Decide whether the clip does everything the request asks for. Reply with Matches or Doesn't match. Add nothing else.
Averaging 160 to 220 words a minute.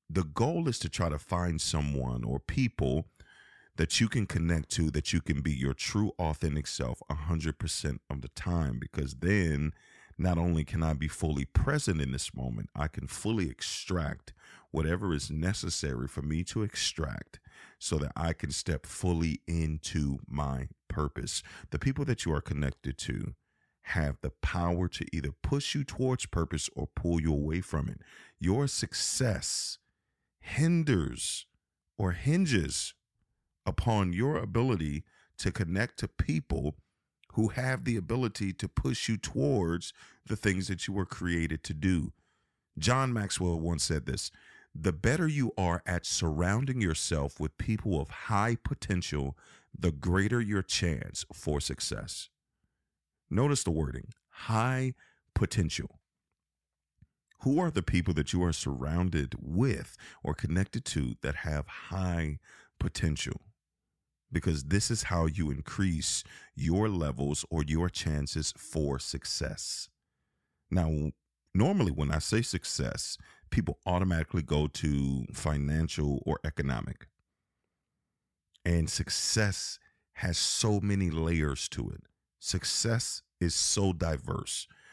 Doesn't match